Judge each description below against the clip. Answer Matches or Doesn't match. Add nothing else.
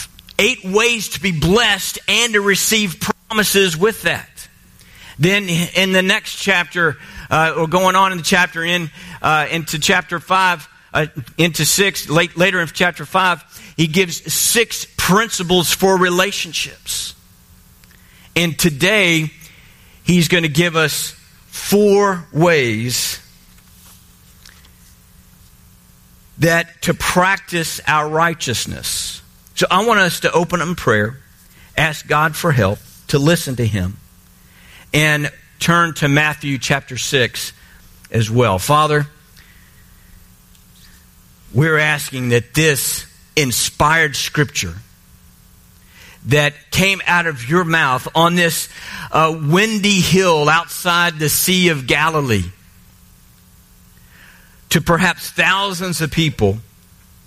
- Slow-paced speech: Matches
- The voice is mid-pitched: Matches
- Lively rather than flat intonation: Doesn't match